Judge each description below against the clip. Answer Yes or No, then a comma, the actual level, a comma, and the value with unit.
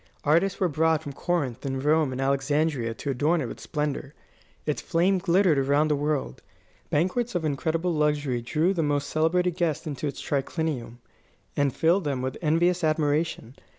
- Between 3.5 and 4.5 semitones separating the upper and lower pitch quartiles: No, average, 3.1 semitones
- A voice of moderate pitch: Yes, medium, 150 Hz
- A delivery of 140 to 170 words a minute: Yes, average, 165 wpm